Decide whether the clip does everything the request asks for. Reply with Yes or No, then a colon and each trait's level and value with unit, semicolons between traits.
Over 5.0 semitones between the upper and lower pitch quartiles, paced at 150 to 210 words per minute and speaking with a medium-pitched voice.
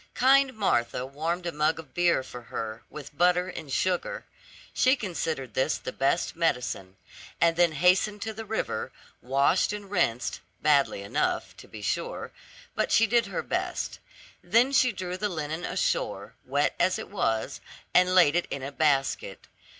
Yes: wide, 5.5 semitones; average, 165 wpm; medium, 165 Hz